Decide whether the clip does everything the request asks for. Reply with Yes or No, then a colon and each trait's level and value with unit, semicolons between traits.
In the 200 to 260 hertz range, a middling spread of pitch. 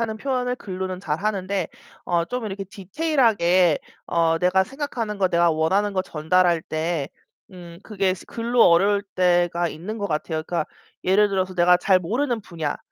No: medium, 185 Hz; average, 3.6 semitones